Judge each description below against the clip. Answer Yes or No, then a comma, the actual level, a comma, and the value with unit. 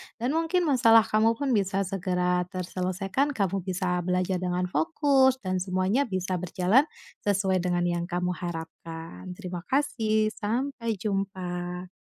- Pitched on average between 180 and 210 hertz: Yes, medium, 185 Hz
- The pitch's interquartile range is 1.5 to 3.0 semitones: No, average, 3.8 semitones